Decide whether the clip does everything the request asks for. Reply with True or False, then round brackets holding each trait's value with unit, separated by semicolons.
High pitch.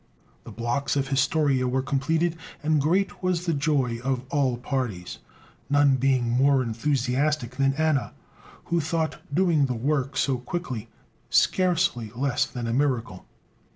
False (135 Hz)